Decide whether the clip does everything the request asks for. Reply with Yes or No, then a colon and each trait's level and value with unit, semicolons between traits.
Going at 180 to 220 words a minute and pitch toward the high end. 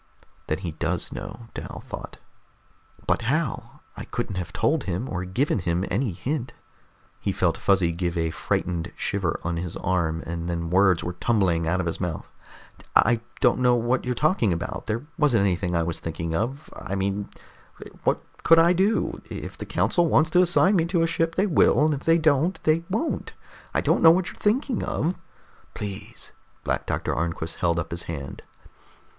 No: average, 185 wpm; low, 105 Hz